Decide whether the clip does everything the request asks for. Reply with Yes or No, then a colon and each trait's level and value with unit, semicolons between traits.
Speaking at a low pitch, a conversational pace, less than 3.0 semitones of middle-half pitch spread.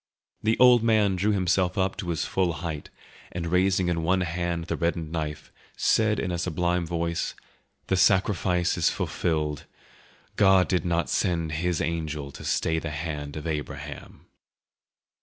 Yes: very low, 85 Hz; average, 155 wpm; narrow, 2.4 semitones